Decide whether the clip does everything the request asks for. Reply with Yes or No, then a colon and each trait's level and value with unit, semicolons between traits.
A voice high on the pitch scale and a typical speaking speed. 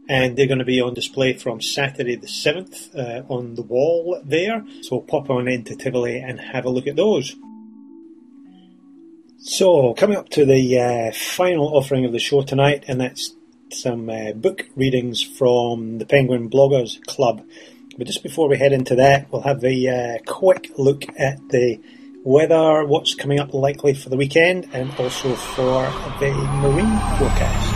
No: low, 135 Hz; average, 175 wpm